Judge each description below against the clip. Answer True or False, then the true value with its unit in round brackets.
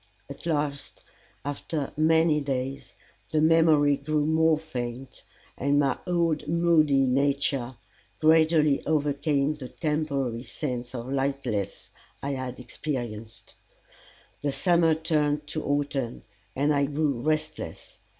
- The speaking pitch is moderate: True (145 Hz)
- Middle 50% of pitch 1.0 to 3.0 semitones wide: True (2.6 semitones)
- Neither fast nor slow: False (110 wpm)